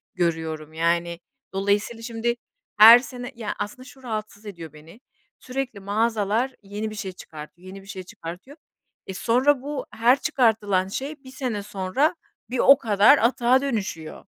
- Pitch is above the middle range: Yes, high, 215 Hz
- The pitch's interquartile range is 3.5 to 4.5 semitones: No, average, 5.0 semitones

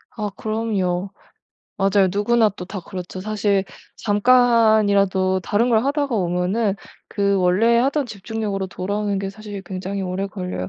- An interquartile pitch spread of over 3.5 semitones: No, average, 2.7 semitones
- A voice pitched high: Yes, high, 200 Hz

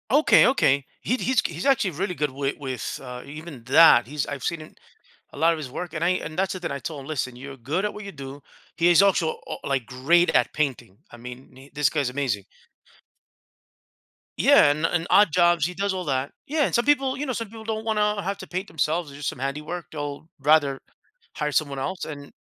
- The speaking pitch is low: No, medium, 155 Hz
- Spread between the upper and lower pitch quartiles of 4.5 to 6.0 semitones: Yes, average, 5.0 semitones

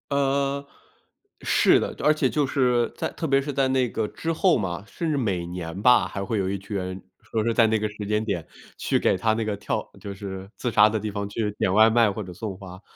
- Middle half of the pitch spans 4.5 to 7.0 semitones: Yes, average, 5.0 semitones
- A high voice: No, low, 110 Hz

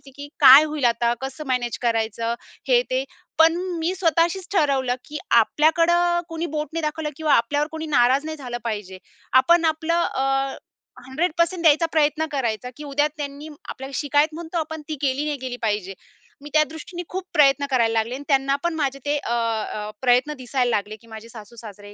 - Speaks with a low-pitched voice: No, very high, 285 Hz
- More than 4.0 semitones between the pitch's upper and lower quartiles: Yes, average, 4.4 semitones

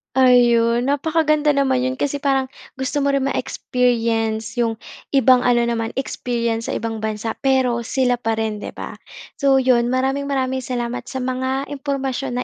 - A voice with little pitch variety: Yes, narrow, 2.3 semitones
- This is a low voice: No, very high, 255 Hz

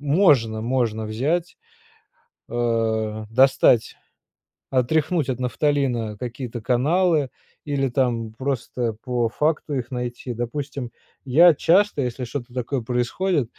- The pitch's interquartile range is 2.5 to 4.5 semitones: Yes, average, 3.5 semitones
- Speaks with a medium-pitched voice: No, low, 125 Hz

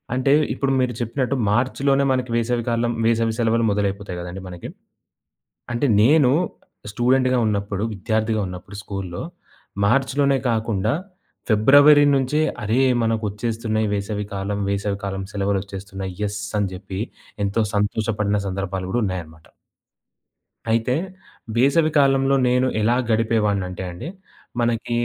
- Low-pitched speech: Yes, low, 110 Hz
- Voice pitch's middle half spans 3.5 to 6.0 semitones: Yes, average, 3.9 semitones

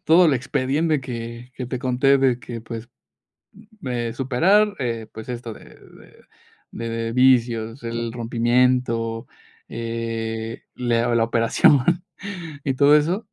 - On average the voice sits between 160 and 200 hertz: No, low, 120 Hz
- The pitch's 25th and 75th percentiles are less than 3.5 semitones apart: Yes, average, 2.7 semitones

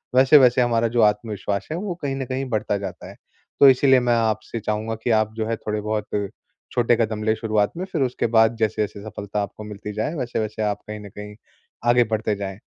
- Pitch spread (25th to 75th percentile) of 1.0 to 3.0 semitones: Yes, narrow, 2.6 semitones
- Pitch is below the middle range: Yes, low, 110 Hz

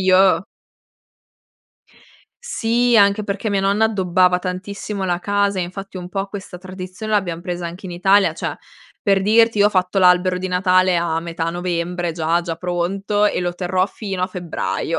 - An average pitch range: No, narrow, 2.1 semitones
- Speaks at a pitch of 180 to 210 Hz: Yes, medium, 185 Hz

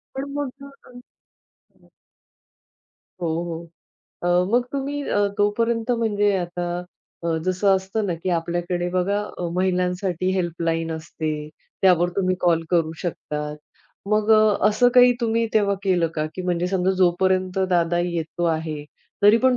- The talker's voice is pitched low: No, medium, 185 Hz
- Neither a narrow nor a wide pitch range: Yes, average, 3.2 semitones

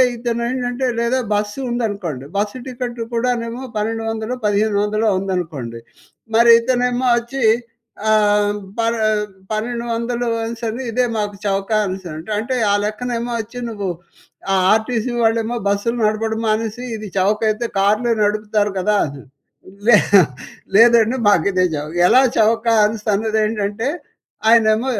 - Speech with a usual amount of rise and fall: No, narrow, 2.3 semitones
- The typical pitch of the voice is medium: No, high, 220 Hz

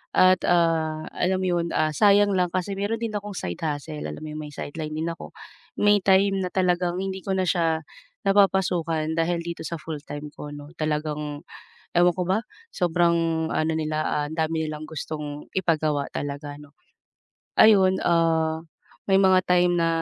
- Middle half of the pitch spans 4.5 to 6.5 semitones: No, average, 3.1 semitones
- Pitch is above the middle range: No, medium, 165 Hz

